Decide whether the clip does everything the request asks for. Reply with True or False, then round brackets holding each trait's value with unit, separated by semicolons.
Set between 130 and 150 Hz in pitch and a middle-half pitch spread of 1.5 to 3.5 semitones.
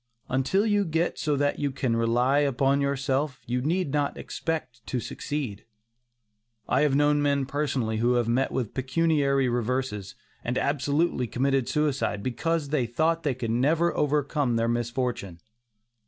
True (135 Hz; 3.2 semitones)